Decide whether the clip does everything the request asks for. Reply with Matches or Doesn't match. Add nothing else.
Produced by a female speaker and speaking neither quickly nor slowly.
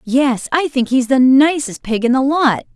Doesn't match